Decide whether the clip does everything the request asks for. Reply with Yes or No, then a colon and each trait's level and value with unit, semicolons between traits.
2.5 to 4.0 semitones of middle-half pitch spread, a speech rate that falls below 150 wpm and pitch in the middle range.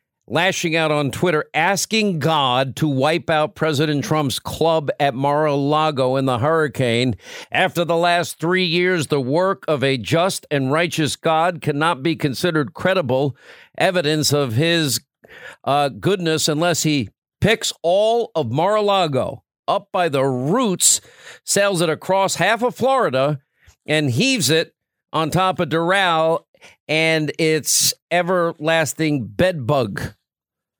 Yes: average, 3.6 semitones; slow, 135 wpm; medium, 160 Hz